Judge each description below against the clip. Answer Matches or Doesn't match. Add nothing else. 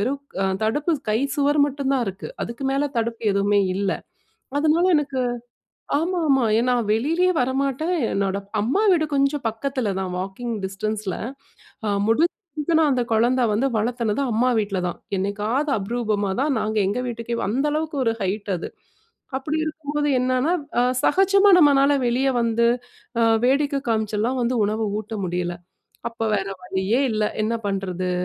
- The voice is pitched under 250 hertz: Matches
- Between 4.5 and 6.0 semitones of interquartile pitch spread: Matches